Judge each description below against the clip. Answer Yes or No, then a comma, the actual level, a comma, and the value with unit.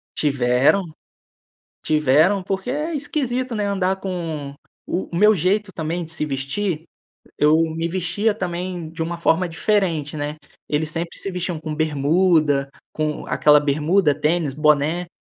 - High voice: No, medium, 165 Hz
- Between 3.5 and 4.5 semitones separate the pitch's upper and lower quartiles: Yes, average, 4.0 semitones